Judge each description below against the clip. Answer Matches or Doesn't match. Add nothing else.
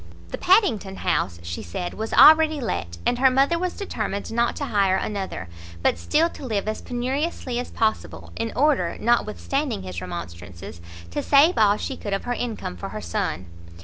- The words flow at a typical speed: Matches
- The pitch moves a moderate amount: Doesn't match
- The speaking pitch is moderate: Doesn't match